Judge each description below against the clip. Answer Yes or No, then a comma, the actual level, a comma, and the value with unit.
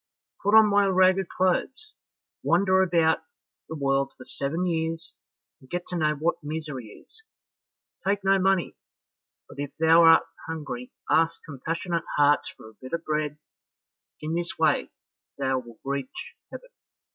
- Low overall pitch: No, medium, 165 Hz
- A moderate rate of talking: Yes, average, 145 wpm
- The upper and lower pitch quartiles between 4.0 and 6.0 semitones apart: Yes, average, 4.4 semitones